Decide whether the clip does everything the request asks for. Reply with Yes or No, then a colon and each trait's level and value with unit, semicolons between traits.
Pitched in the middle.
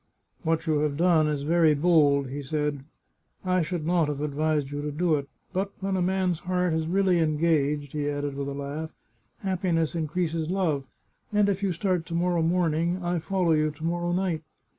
Yes: medium, 160 Hz